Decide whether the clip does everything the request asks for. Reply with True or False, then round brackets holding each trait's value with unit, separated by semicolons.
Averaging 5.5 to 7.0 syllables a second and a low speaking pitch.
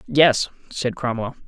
False (3.9 syllables/s; 130 Hz)